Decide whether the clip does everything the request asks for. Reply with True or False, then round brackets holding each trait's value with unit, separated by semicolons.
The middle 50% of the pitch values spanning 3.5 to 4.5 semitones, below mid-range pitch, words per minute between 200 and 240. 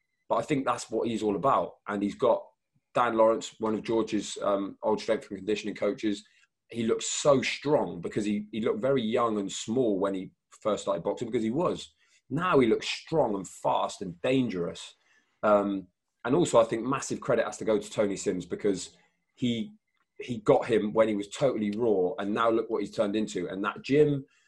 False (2.5 semitones; 110 Hz; 205 wpm)